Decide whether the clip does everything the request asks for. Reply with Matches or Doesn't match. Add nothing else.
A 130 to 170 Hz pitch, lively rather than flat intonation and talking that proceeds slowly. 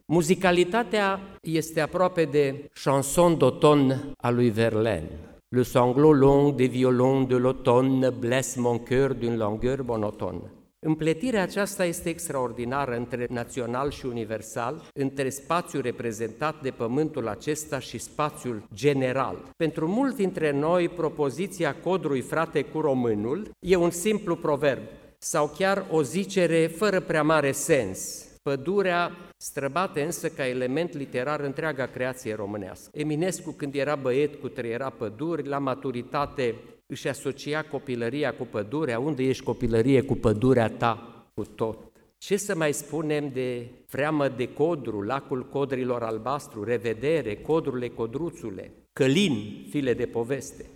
Doesn't match